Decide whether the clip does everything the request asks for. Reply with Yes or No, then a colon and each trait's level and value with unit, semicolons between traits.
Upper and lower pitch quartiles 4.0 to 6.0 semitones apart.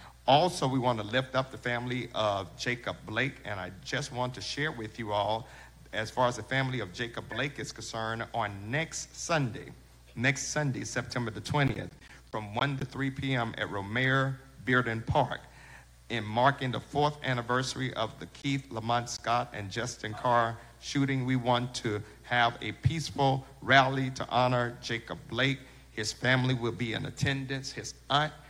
No: average, 3.0 semitones